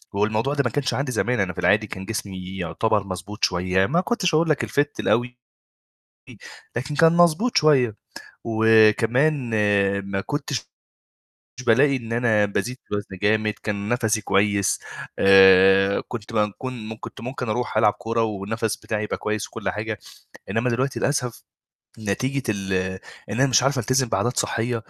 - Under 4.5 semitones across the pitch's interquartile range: Yes, average, 3.9 semitones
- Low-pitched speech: Yes, low, 115 Hz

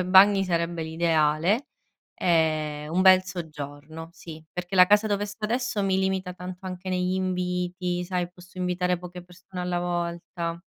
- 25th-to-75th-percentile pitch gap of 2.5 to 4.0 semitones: No, narrow, 1.8 semitones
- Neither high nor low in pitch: Yes, medium, 180 Hz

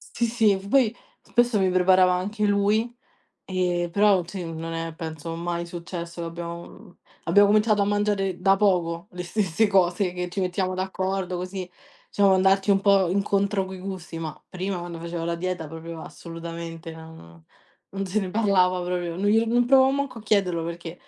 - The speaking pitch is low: No, medium, 185 Hz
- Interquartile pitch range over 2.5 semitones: Yes, average, 2.9 semitones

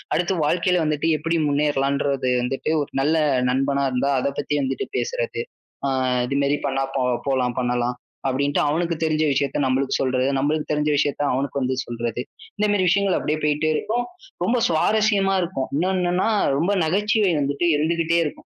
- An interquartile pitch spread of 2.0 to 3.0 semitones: No, average, 4.4 semitones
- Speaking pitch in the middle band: Yes, medium, 150 Hz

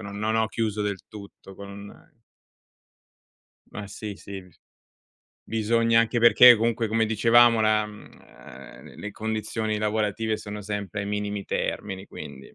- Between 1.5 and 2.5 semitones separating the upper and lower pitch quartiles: Yes, narrow, 1.8 semitones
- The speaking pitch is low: Yes, low, 105 Hz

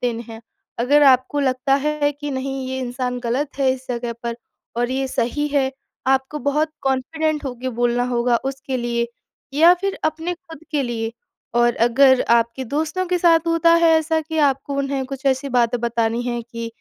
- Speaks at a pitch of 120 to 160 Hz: No, very high, 265 Hz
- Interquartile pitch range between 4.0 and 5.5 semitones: No, average, 3.5 semitones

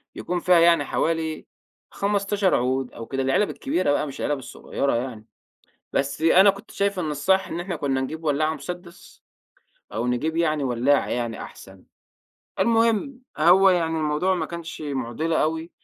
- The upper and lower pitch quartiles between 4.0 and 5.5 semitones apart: Yes, average, 4.8 semitones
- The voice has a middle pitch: Yes, medium, 160 Hz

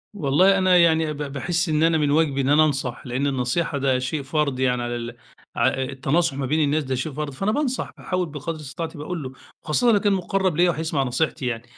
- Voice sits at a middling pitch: Yes, medium, 150 Hz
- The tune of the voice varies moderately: Yes, average, 3.9 semitones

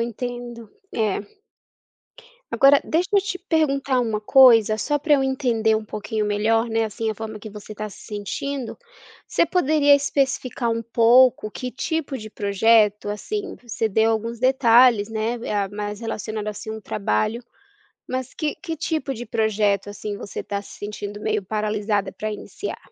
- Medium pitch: No, high, 225 Hz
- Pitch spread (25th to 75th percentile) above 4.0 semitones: No, average, 3.6 semitones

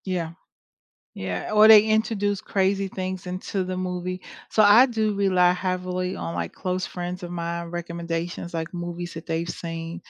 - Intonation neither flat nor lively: No, narrow, 2.1 semitones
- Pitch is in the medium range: Yes, medium, 180 Hz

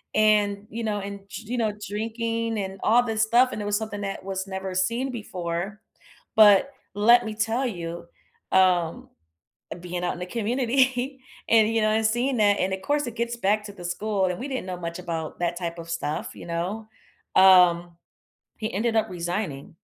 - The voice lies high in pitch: Yes, high, 205 Hz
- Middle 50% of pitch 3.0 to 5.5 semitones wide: Yes, average, 3.9 semitones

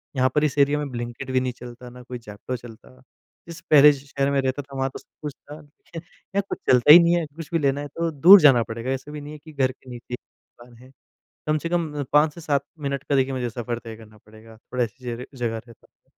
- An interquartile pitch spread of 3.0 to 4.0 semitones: Yes, average, 3.4 semitones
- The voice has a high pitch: No, low, 135 Hz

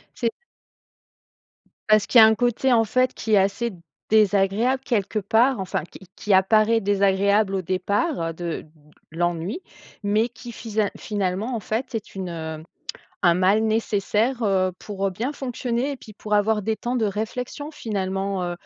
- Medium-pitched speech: No, high, 210 Hz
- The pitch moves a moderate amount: Yes, average, 3.3 semitones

